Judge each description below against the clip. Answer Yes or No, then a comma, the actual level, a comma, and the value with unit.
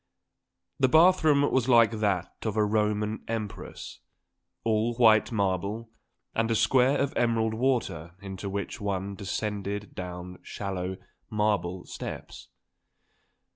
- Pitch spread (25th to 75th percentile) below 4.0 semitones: Yes, average, 2.8 semitones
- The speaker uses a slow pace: Yes, slow, 120 wpm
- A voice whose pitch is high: No, low, 105 Hz